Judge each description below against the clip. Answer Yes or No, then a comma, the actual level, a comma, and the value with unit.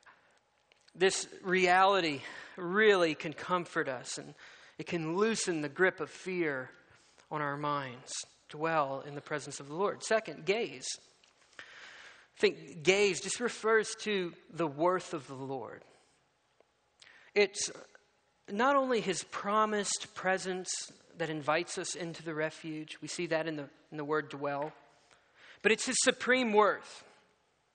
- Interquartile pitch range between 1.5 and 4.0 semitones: No, average, 5.0 semitones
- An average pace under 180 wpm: Yes, slow, 135 wpm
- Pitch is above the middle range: No, medium, 175 Hz